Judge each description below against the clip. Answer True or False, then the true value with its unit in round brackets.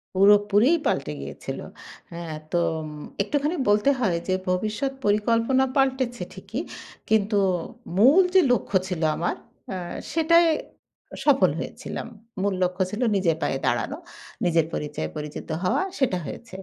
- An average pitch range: False (6.3 semitones)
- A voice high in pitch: True (210 Hz)